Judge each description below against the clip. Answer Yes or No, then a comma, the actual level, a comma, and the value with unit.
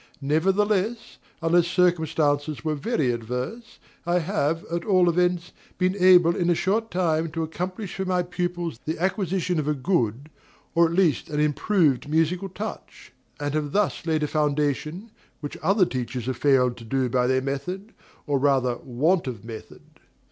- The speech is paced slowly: No, average, 160 wpm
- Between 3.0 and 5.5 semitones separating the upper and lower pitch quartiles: Yes, average, 4.3 semitones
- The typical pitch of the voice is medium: Yes, medium, 165 Hz